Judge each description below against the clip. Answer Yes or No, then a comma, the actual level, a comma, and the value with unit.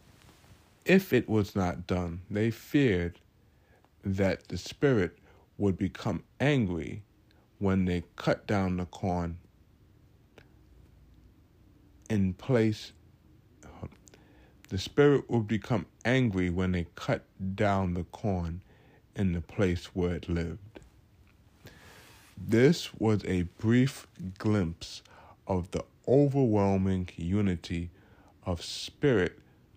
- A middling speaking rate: No, slow, 100 wpm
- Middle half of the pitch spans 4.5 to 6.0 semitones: No, average, 3.2 semitones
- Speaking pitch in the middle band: No, low, 100 Hz